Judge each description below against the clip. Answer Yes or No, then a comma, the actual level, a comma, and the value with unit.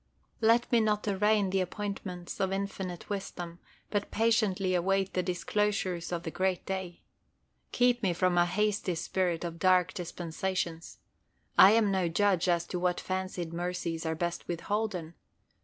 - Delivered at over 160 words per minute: No, average, 150 wpm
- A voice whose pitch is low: No, medium, 185 Hz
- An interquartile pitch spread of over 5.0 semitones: No, average, 2.7 semitones